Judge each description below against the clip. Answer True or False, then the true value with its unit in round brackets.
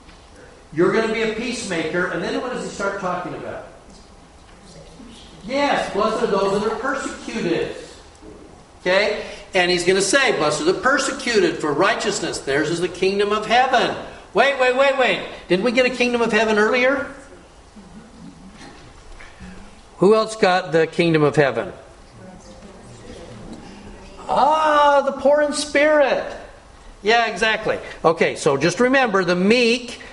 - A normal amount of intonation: False (5.8 semitones)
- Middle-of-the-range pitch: False (225 Hz)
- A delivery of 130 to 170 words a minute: True (140 wpm)